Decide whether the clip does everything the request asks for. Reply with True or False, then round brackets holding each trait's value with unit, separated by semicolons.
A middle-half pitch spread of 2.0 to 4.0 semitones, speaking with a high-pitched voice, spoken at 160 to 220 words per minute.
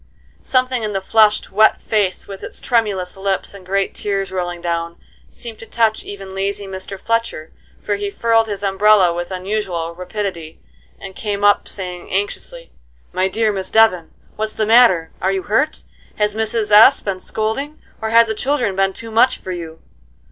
True (2.8 semitones; 200 Hz; 175 wpm)